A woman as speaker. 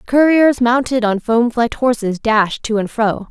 Yes: female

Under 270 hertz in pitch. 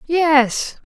No: very high, 305 Hz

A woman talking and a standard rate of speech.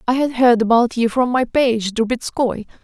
Yes: female; average, 190 wpm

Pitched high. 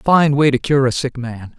No: low, 135 Hz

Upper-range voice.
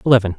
No: low, 110 Hz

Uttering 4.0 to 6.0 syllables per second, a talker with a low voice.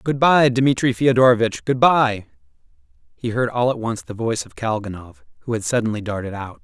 Yes: 5.5 syllables/s; low, 115 Hz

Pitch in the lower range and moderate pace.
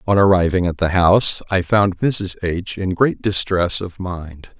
Yes: very low, 90 Hz; average, 185 wpm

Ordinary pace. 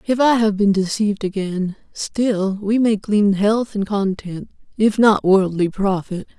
Yes: average, 160 wpm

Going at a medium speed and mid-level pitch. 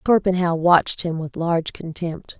Yes: average, 150 wpm; medium, 170 Hz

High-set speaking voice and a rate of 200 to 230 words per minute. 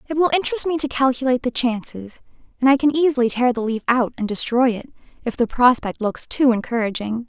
Yes: very high, 250 Hz; fast, 205 wpm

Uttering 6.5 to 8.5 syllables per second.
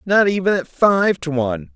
No: 5.0 syllables/s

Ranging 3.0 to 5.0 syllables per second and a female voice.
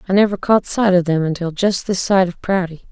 No: 5.5 syllables/s; female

